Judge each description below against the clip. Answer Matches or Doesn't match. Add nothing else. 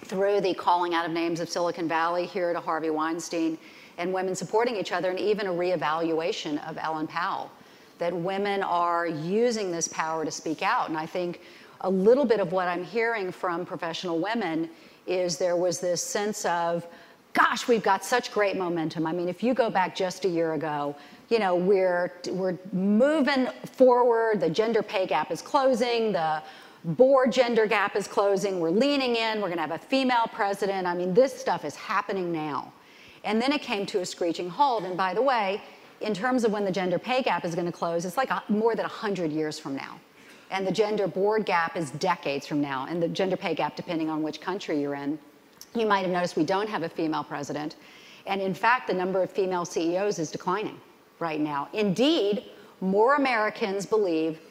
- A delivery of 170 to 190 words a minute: Doesn't match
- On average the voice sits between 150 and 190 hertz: Matches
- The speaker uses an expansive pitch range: Doesn't match